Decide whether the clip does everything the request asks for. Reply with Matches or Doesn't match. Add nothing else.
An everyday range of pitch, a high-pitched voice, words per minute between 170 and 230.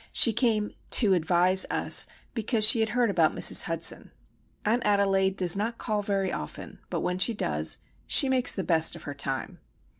Matches